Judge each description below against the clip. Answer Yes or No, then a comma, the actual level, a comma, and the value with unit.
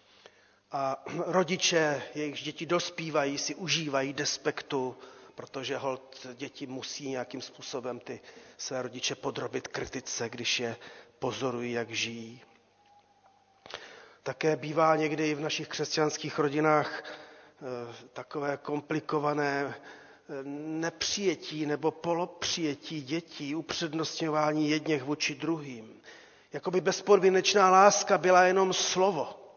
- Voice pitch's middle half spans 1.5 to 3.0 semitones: No, average, 3.4 semitones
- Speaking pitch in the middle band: Yes, medium, 150 Hz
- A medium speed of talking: No, slow, 100 wpm